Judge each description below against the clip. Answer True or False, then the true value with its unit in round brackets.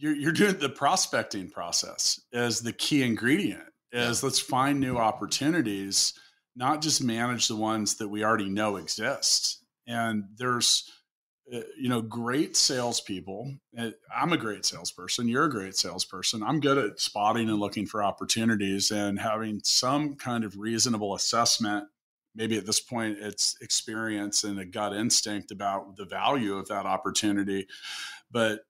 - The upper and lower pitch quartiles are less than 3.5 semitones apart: True (2.9 semitones)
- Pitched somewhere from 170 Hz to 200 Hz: False (110 Hz)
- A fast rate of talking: False (145 wpm)